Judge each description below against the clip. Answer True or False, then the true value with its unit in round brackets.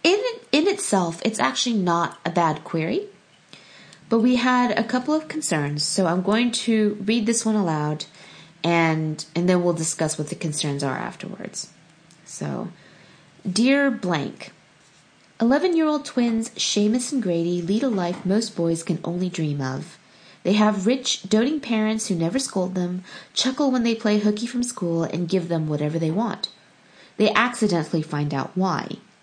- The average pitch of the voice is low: False (190 Hz)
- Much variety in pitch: True (5.9 semitones)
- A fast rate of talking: False (160 wpm)